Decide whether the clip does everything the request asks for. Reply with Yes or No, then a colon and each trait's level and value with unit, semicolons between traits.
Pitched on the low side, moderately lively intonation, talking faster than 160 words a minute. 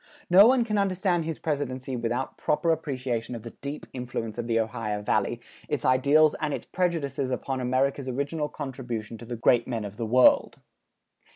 Yes: low, 130 Hz; average, 4.3 semitones; average, 175 wpm